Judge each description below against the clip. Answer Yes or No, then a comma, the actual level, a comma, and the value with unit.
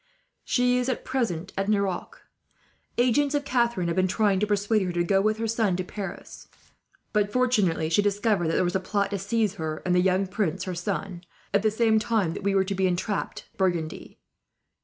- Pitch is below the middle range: No, high, 200 Hz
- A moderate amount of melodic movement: Yes, average, 3.1 semitones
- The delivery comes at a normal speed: No, fast, 210 wpm